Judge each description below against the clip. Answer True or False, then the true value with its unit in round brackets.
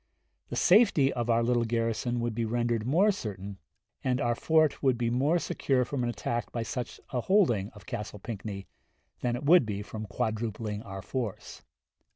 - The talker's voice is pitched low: True (120 Hz)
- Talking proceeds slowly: False (180 wpm)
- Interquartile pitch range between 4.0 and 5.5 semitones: False (3.1 semitones)